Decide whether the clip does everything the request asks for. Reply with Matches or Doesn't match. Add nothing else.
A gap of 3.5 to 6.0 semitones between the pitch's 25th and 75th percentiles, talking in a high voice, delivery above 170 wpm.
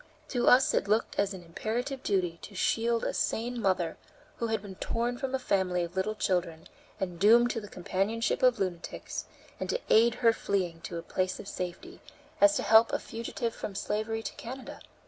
Matches